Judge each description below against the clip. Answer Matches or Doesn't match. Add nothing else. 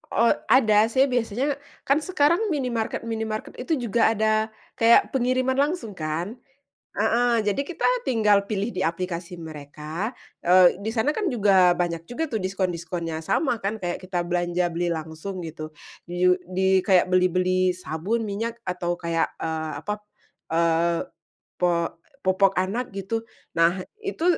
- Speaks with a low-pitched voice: Doesn't match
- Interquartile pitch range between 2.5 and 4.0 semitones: Doesn't match